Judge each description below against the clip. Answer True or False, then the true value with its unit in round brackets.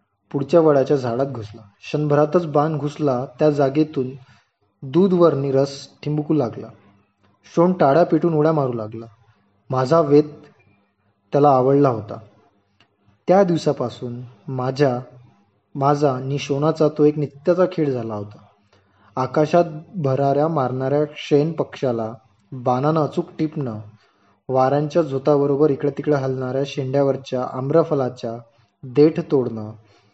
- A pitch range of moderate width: True (4.7 semitones)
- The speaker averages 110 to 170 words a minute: False (100 wpm)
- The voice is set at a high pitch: False (135 Hz)